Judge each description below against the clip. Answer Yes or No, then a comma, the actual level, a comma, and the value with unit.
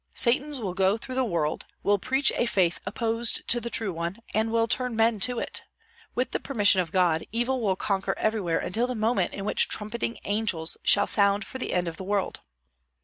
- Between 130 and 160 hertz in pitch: No, high, 215 Hz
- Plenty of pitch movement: No, average, 3.9 semitones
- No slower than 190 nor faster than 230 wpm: Yes, fast, 205 wpm